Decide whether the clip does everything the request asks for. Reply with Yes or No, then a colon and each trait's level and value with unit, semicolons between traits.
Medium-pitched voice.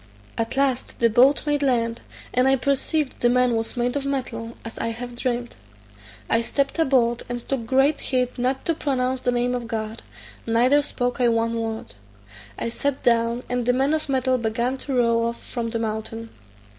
No: high, 245 Hz